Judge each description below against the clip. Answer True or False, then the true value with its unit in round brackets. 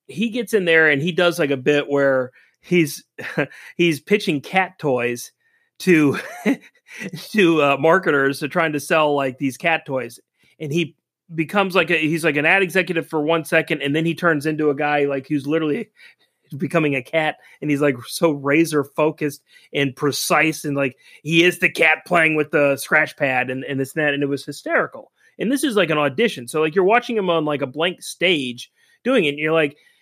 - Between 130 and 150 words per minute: False (205 wpm)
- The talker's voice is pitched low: False (155 Hz)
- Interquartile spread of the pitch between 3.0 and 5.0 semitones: True (3.3 semitones)